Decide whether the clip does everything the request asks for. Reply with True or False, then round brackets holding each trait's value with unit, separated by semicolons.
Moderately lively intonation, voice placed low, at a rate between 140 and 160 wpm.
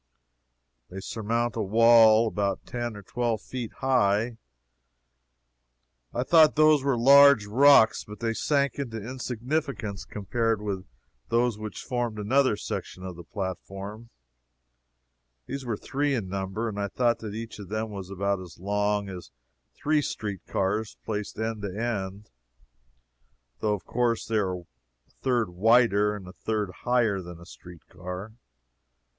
True (3.2 semitones; 110 Hz; 145 wpm)